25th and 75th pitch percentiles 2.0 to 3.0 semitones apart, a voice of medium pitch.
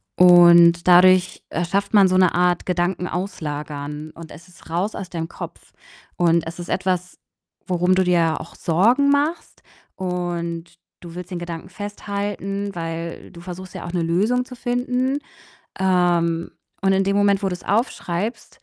Yes: narrow, 2.5 semitones; medium, 180 Hz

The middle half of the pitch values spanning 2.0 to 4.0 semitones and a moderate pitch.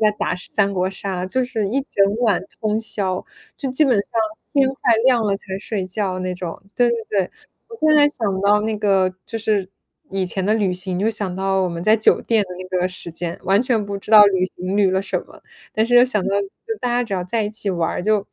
No: average, 3.0 semitones; high, 200 Hz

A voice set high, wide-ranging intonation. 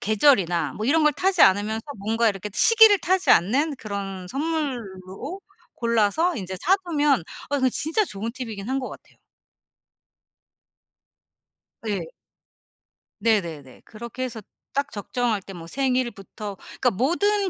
Yes: high, 235 Hz; wide, 6.6 semitones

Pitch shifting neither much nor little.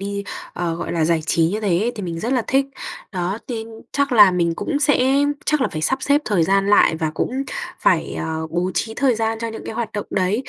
No: wide, 6.2 semitones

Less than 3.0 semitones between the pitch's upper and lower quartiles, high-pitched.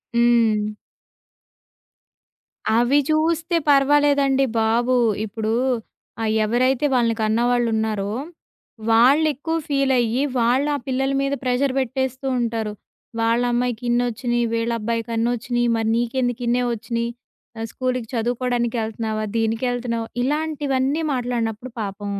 Yes: narrow, 2.4 semitones; high, 240 Hz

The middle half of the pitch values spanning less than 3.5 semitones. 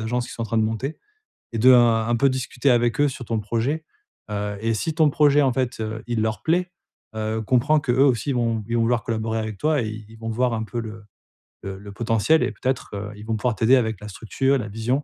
Yes: average, 2.9 semitones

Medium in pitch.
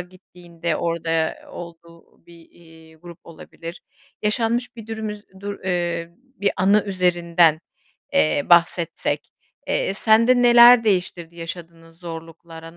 Yes: medium, 175 Hz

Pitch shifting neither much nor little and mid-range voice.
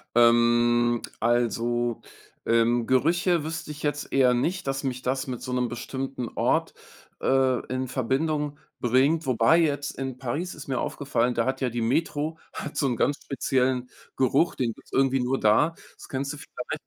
No: average, 3.1 semitones; low, 130 Hz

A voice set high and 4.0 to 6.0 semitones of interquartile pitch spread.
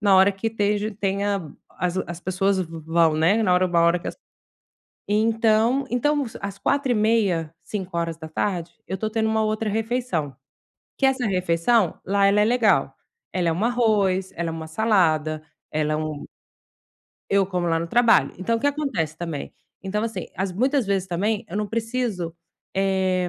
Yes: high, 195 Hz; average, 4.5 semitones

